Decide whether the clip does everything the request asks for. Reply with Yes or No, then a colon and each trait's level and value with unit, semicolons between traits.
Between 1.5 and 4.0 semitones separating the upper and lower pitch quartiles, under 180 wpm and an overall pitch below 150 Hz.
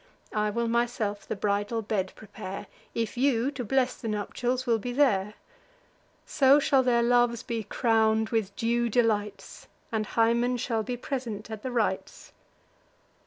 No: narrow, 2.6 semitones; average, 150 wpm; high, 230 Hz